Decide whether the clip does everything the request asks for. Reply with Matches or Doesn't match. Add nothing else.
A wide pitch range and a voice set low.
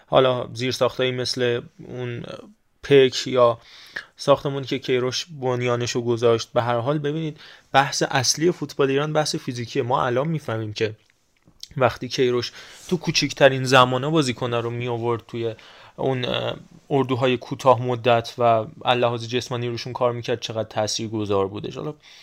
Doesn't match